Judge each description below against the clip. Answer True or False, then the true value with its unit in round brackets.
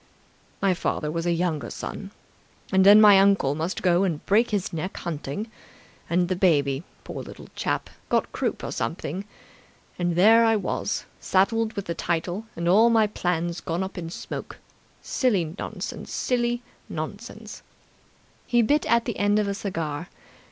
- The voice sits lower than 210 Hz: True (185 Hz)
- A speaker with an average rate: True (160 wpm)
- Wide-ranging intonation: False (4.1 semitones)